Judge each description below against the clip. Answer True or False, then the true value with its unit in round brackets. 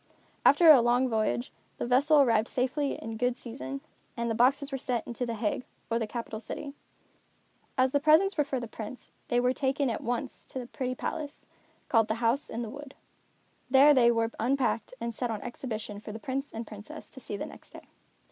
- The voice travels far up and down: False (3.2 semitones)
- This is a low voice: False (245 Hz)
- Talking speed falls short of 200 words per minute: False (205 wpm)